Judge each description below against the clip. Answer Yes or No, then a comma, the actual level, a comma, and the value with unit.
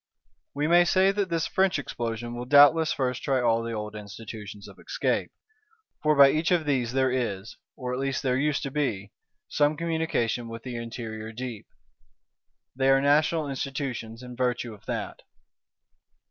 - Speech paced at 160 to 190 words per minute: Yes, average, 165 wpm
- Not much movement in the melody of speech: No, average, 4.3 semitones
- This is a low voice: Yes, low, 130 Hz